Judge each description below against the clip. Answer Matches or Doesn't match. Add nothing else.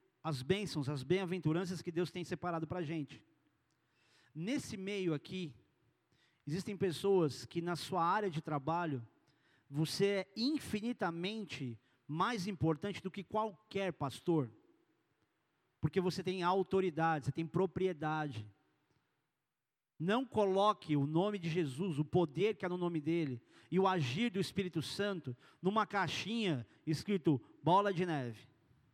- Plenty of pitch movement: Doesn't match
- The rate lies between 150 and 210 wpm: Doesn't match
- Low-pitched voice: Doesn't match